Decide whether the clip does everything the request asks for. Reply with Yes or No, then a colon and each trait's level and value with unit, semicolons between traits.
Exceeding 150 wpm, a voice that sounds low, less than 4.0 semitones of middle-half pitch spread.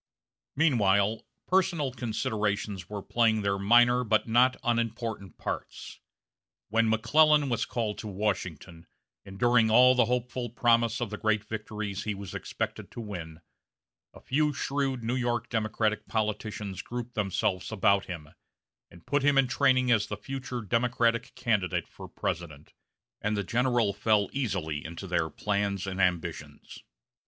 No: average, 145 wpm; low, 110 Hz; average, 3.6 semitones